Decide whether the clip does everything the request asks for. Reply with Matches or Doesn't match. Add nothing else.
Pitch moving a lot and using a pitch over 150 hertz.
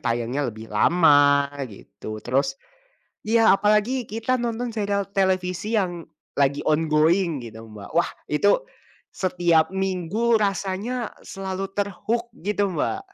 Matches